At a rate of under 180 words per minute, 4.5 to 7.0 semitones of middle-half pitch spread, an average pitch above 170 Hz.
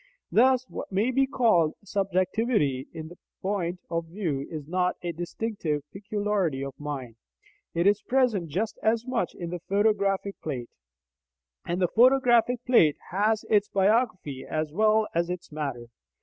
Yes: average, 150 wpm; average, 5.2 semitones; high, 190 Hz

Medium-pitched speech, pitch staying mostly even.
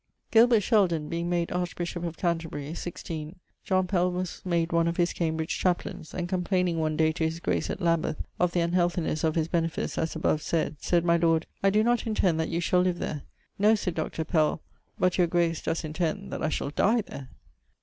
Yes: medium, 170 Hz; narrow, 2.0 semitones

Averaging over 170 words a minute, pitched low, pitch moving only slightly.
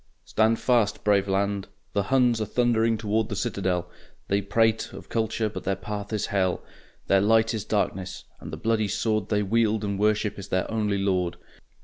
Yes: average, 180 wpm; low, 105 Hz; narrow, 2.2 semitones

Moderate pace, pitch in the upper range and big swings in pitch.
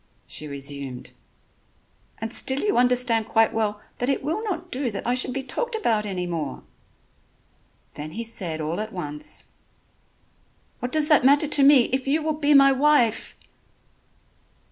Yes: average, 160 wpm; high, 245 Hz; wide, 7.1 semitones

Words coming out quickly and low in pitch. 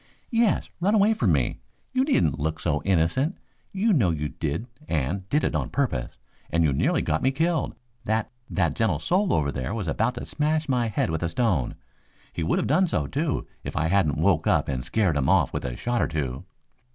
Yes: fast, 215 wpm; low, 100 Hz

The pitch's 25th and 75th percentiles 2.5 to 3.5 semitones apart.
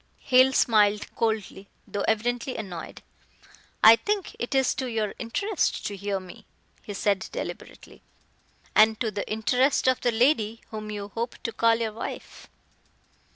Yes: average, 3.1 semitones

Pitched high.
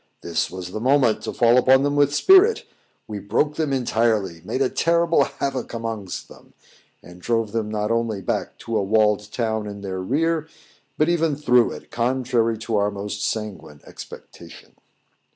No: low, 115 Hz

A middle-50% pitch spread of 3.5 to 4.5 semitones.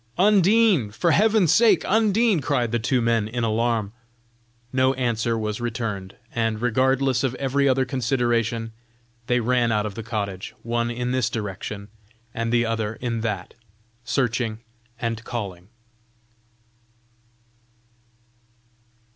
No: average, 2.7 semitones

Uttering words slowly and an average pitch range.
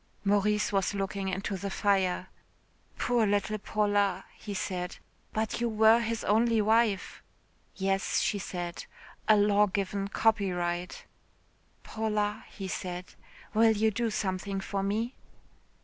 No: slow, 130 wpm; narrow, 2.1 semitones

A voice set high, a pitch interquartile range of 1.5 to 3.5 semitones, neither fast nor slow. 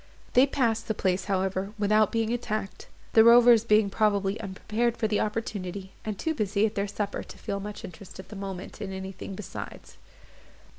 Yes: high, 210 Hz; narrow, 2.4 semitones; average, 180 wpm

